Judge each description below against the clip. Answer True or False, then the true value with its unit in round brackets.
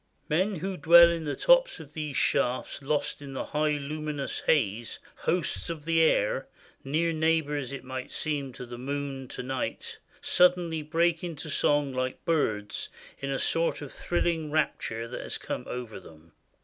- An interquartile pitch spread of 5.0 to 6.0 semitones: False (3.7 semitones)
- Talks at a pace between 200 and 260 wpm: False (165 wpm)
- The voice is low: False (150 Hz)